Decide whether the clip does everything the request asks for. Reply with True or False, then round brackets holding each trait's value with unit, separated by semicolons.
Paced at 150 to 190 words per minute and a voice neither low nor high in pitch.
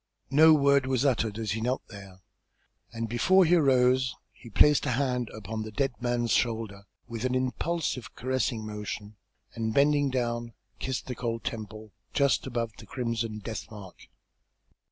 False (155 wpm; 120 Hz)